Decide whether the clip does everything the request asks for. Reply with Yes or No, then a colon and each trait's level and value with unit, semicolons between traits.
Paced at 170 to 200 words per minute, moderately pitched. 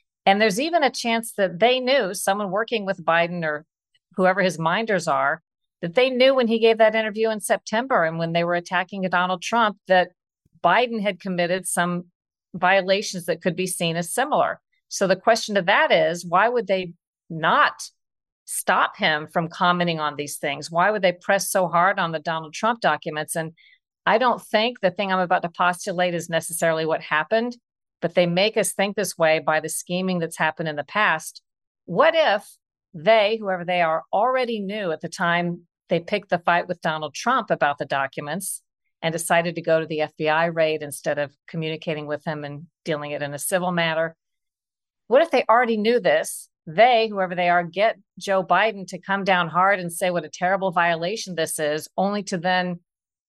Yes: average, 195 wpm; medium, 180 Hz